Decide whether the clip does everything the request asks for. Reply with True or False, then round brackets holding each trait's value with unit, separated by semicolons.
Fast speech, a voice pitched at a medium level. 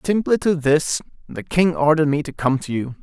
True (220 wpm; 155 Hz)